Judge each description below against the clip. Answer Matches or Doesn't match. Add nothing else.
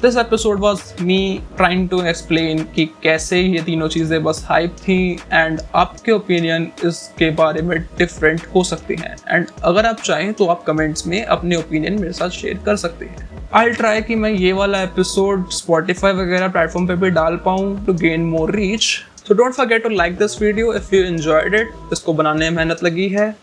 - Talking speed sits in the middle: Doesn't match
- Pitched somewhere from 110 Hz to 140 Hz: Doesn't match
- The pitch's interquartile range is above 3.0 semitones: Matches